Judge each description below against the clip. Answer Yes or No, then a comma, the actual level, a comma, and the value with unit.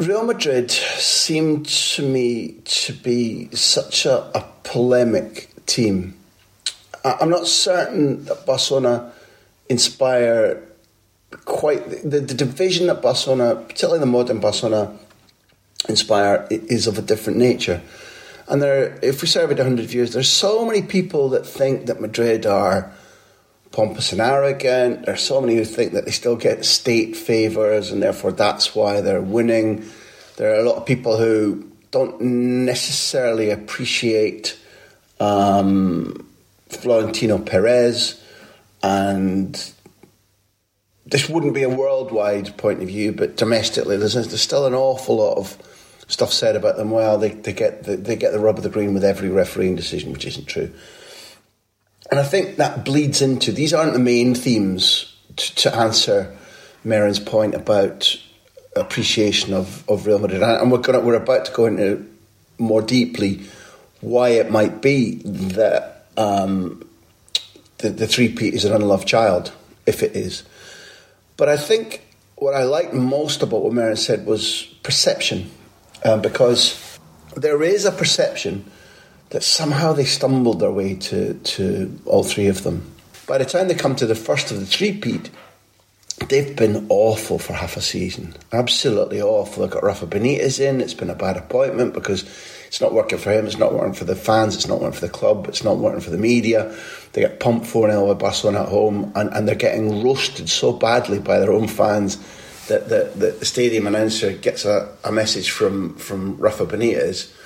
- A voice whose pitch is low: Yes, low, 120 Hz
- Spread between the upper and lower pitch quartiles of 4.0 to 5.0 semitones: Yes, average, 4.7 semitones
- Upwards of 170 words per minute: No, average, 165 wpm